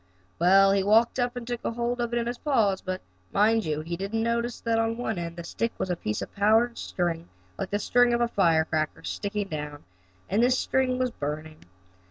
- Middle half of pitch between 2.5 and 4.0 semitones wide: No, wide, 5.5 semitones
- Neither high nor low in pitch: No, high, 210 Hz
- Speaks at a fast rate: Yes, fast, 220 wpm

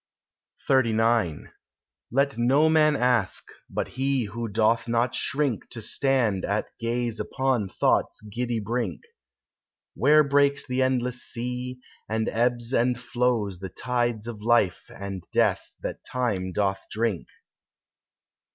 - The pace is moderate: No, slow, 125 wpm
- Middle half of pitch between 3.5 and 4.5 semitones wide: No, average, 2.7 semitones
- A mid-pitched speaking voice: No, low, 120 Hz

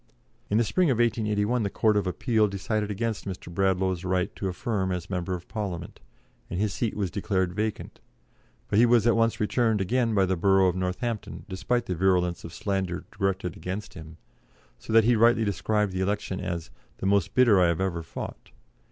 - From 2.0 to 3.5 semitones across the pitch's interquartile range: Yes, average, 3.1 semitones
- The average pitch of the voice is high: No, low, 100 Hz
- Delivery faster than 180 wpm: Yes, average, 195 wpm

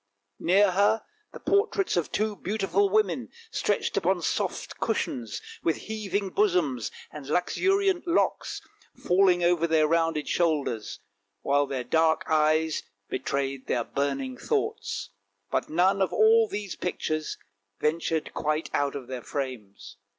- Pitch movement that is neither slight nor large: No, wide, 6.1 semitones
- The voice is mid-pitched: Yes, medium, 165 Hz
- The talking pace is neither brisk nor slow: No, slow, 130 wpm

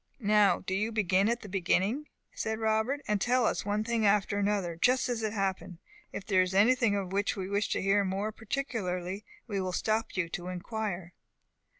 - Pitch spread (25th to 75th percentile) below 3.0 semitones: Yes, narrow, 2.6 semitones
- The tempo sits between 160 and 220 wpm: Yes, average, 195 wpm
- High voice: Yes, high, 205 Hz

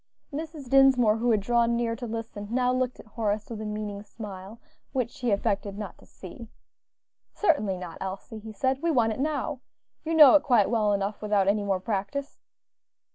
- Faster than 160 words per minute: Yes, average, 185 wpm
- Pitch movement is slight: No, average, 3.8 semitones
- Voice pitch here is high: Yes, high, 225 Hz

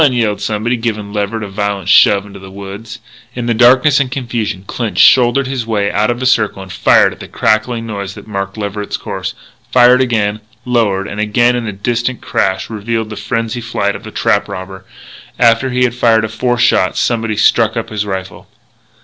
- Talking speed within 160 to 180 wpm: No, average, 195 wpm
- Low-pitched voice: Yes, low, 110 Hz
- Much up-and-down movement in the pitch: No, average, 3.0 semitones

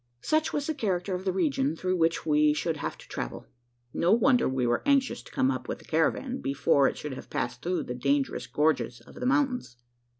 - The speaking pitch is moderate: Yes, medium, 165 Hz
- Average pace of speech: No, fast, 220 wpm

